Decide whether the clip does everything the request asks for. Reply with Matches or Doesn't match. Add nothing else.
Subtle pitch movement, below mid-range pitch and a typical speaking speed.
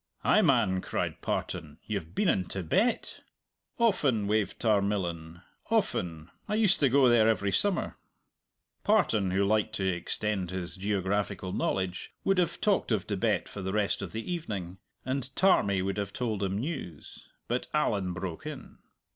Doesn't match